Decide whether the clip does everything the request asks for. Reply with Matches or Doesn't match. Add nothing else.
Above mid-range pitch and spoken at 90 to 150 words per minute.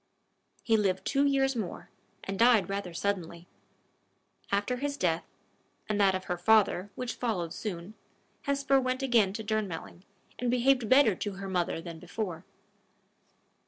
Matches